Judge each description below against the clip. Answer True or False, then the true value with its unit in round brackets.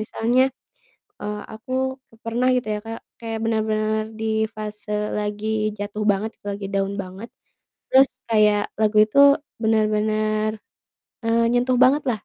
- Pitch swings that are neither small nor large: False (1.4 semitones)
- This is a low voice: False (215 Hz)